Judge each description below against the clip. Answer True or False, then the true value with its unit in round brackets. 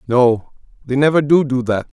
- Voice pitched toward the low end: True (130 Hz)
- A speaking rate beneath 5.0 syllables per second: True (4.8 syllables/s)